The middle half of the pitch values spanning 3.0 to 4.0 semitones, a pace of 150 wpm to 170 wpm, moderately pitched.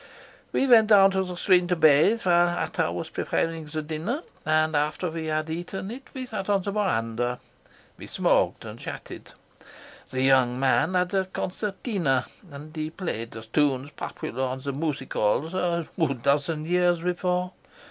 No: average, 4.6 semitones; average, 165 wpm; medium, 165 Hz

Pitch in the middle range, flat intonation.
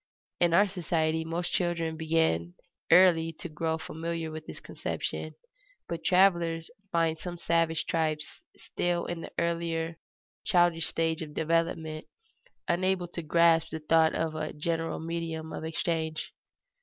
Yes: medium, 165 Hz; narrow, 1.1 semitones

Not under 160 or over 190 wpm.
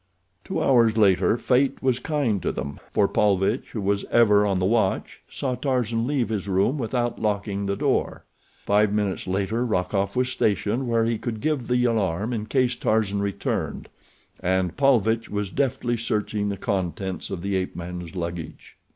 Yes: average, 170 wpm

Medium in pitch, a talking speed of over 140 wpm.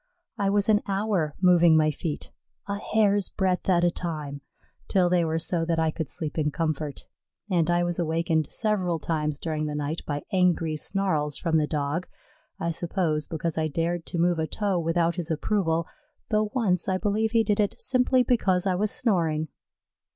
Yes: medium, 170 Hz; average, 185 wpm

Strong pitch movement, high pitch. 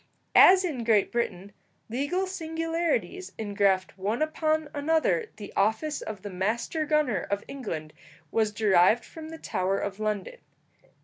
Yes: wide, 7.7 semitones; high, 235 Hz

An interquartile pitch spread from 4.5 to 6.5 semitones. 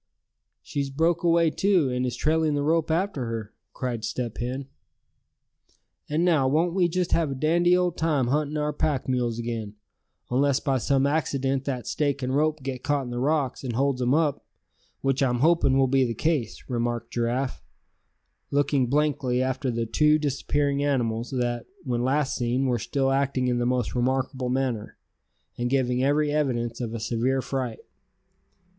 No: average, 3.3 semitones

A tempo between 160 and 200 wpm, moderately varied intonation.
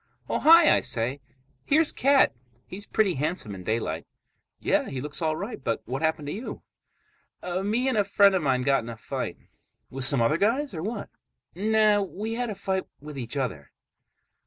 No: average, 185 wpm; wide, 8.2 semitones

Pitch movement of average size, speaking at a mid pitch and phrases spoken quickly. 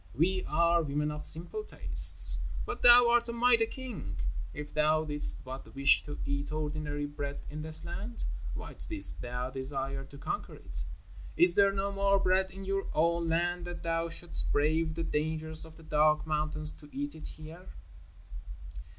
No: average, 4.0 semitones; medium, 160 Hz; average, 170 wpm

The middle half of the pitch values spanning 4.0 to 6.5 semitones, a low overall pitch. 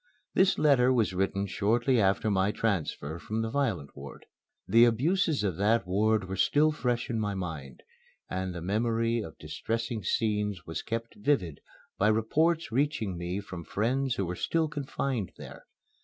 Yes: average, 4.5 semitones; low, 110 Hz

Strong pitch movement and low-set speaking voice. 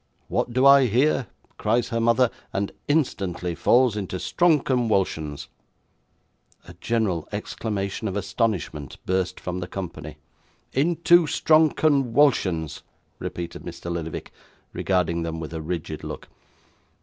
Yes: wide, 7.0 semitones; low, 100 Hz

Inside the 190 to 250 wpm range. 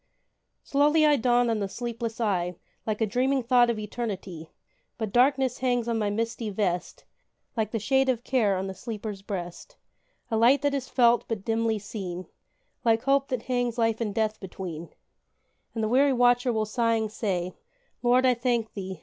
No: average, 175 wpm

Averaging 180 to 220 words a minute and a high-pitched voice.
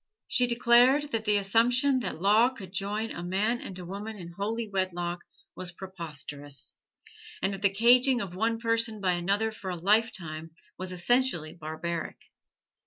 No: average, 160 wpm; high, 200 Hz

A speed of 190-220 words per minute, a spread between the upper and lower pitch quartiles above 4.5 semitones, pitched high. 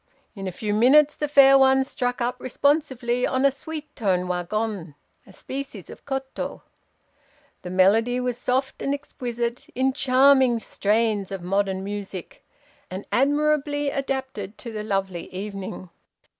No: average, 140 wpm; wide, 5.4 semitones; high, 245 Hz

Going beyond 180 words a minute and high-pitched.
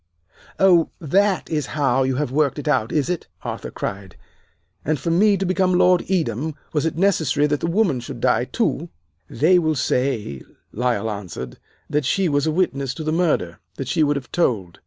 No: average, 190 wpm; medium, 150 Hz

